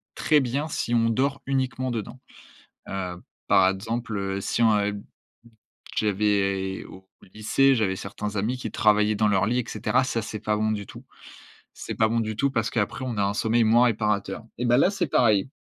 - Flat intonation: No, average, 3.2 semitones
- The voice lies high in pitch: No, low, 110 Hz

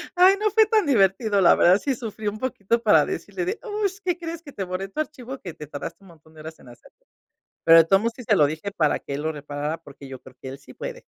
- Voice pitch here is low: No, high, 200 Hz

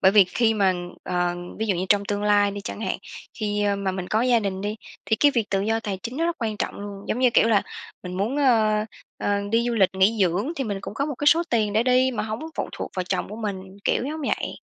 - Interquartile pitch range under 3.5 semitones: Yes, average, 2.9 semitones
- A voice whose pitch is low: No, high, 210 Hz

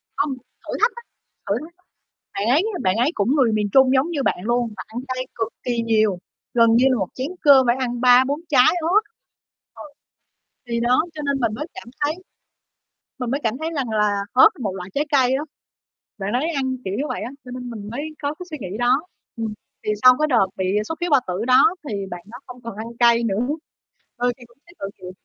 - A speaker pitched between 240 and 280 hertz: Yes, high, 245 Hz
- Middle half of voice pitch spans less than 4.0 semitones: Yes, average, 3.6 semitones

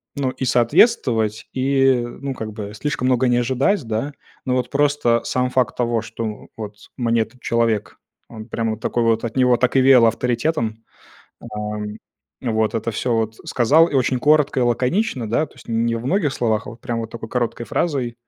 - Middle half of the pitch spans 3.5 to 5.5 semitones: No, narrow, 2.6 semitones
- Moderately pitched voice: No, low, 120 Hz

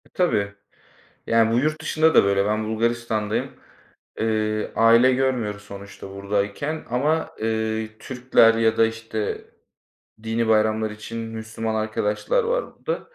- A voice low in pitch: Yes, low, 110 Hz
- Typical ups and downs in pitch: No, narrow, 2.2 semitones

